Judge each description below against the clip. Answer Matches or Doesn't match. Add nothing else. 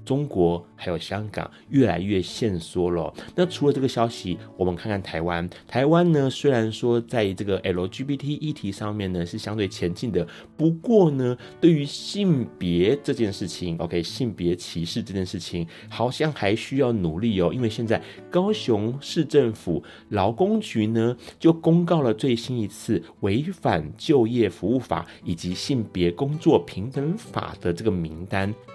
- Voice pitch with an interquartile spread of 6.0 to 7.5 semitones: Matches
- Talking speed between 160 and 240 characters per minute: Doesn't match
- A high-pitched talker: Doesn't match